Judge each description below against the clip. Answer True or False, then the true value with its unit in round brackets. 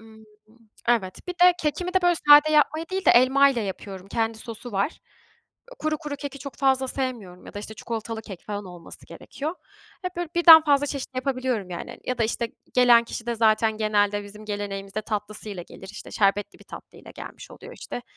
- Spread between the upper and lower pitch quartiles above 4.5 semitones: True (5.5 semitones)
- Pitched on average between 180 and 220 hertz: False (235 Hz)